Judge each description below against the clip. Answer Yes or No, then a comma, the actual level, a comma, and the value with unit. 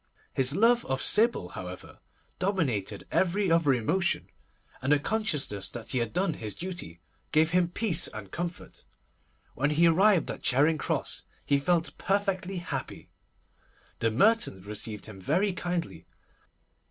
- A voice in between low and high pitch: Yes, medium, 160 Hz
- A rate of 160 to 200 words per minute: No, average, 140 wpm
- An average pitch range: No, wide, 8.3 semitones